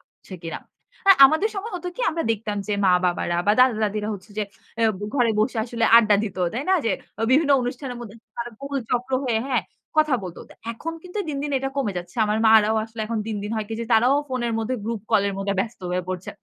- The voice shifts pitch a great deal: No, average, 4.0 semitones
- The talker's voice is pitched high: Yes, high, 230 Hz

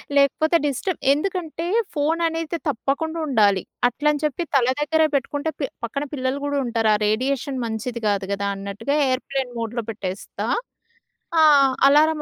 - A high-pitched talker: Yes, very high, 275 Hz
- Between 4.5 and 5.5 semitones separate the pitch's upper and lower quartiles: Yes, average, 4.9 semitones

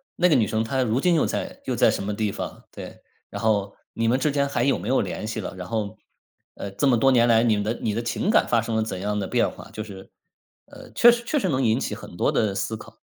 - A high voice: No, low, 115 Hz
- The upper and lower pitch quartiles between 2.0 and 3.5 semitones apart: No, average, 4.0 semitones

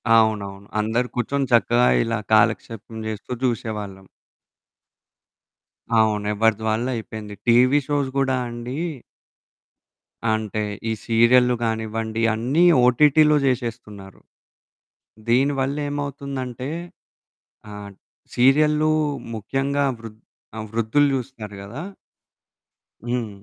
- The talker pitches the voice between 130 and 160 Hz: No, low, 120 Hz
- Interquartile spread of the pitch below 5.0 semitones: Yes, average, 3.4 semitones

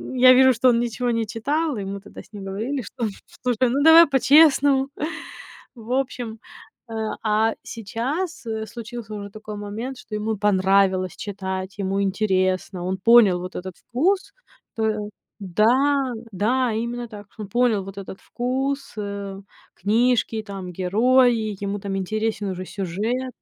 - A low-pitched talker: No, high, 220 Hz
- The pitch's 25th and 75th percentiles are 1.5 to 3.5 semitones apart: No, average, 4.0 semitones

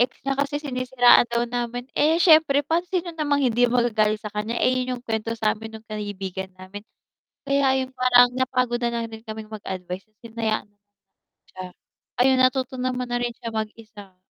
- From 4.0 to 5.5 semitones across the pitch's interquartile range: No, average, 3.0 semitones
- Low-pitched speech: No, high, 240 Hz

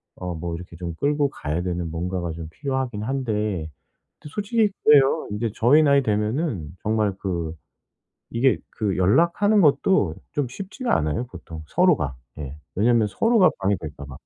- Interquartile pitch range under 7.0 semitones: No, wide, 8.7 semitones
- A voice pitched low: Yes, low, 105 Hz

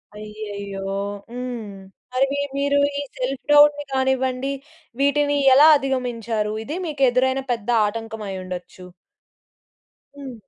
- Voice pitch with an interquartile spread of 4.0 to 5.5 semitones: Yes, average, 4.5 semitones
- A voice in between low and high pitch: No, very high, 255 Hz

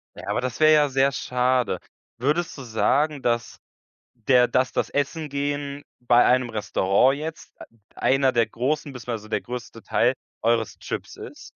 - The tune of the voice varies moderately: Yes, average, 3.1 semitones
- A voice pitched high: No, low, 130 Hz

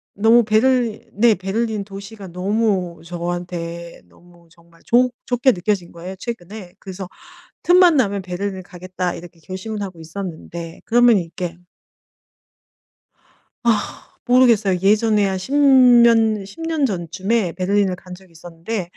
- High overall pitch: Yes, high, 195 Hz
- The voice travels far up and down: No, average, 4.3 semitones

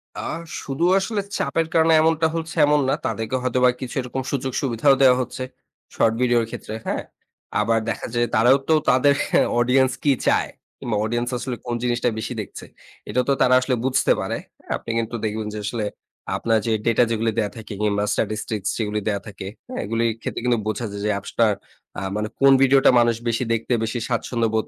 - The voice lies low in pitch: Yes, low, 120 Hz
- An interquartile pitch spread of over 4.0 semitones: No, average, 3.0 semitones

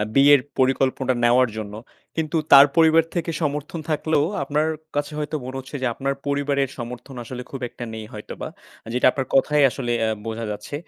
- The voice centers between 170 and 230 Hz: No, low, 135 Hz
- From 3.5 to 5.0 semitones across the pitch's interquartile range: No, average, 2.7 semitones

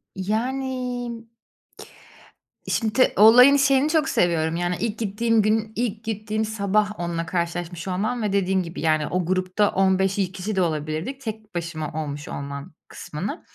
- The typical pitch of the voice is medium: No, high, 200 Hz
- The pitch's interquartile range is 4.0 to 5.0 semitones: Yes, average, 4.4 semitones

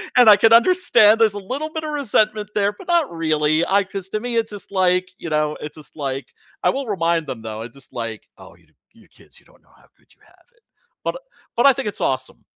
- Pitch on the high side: Yes, high, 200 Hz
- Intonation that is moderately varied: No, wide, 7.0 semitones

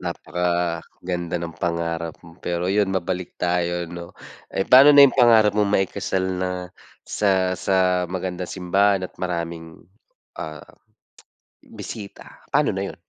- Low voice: Yes, very low, 90 Hz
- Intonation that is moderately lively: No, narrow, 2.0 semitones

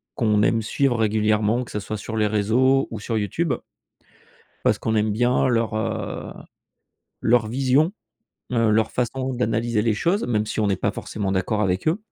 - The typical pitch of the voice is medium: No, low, 110 Hz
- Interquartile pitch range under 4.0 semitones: Yes, average, 2.7 semitones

